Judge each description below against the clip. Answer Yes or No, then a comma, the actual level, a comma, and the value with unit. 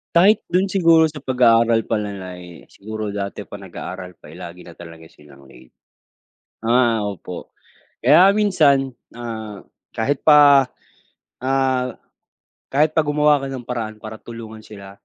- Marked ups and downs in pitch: Yes, wide, 6.0 semitones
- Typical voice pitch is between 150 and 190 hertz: No, low, 115 Hz